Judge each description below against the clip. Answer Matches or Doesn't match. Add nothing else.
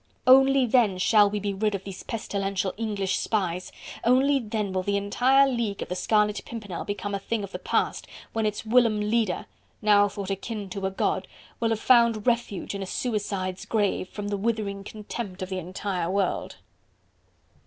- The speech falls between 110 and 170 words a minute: Doesn't match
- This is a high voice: Matches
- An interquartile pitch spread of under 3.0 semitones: Matches